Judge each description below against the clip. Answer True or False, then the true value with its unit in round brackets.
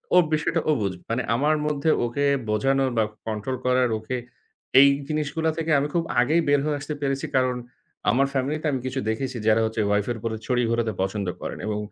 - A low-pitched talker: True (130 Hz)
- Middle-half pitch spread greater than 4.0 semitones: True (4.4 semitones)